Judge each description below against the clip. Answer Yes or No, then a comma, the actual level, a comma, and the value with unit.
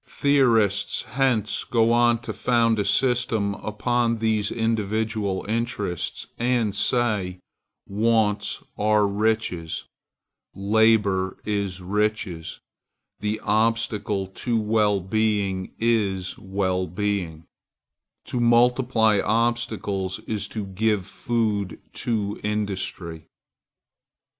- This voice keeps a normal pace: No, slow, 90 wpm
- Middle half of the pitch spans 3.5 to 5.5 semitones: No, narrow, 2.5 semitones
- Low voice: Yes, low, 105 Hz